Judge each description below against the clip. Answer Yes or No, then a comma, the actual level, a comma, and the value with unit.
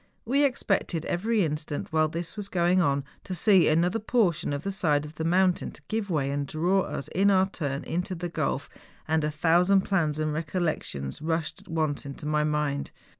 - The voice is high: No, medium, 165 Hz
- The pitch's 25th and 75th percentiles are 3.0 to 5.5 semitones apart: Yes, average, 3.8 semitones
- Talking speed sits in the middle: Yes, average, 190 wpm